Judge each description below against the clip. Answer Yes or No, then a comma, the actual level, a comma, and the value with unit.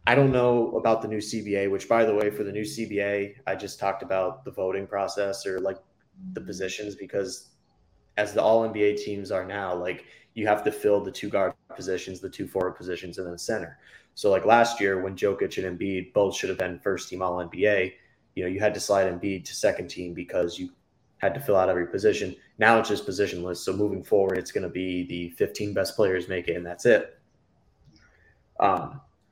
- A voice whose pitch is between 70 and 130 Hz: Yes, low, 100 Hz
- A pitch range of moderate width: No, narrow, 2.3 semitones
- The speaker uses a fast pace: Yes, fast, 215 wpm